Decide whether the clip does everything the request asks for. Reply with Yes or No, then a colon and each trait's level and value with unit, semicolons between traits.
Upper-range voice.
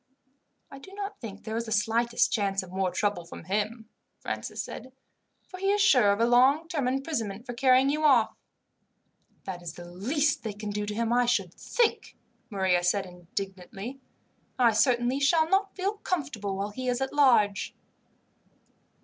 Yes: high, 235 Hz